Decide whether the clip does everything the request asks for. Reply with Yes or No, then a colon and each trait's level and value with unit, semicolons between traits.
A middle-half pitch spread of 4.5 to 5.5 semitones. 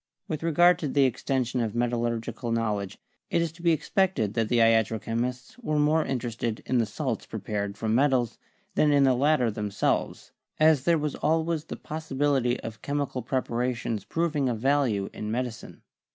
Yes: average, 4.8 semitones